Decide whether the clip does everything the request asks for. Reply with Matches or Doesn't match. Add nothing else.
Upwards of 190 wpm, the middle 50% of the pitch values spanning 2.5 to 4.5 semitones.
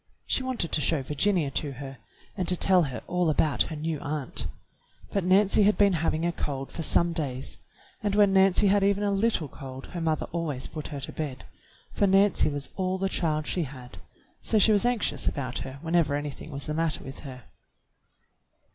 Doesn't match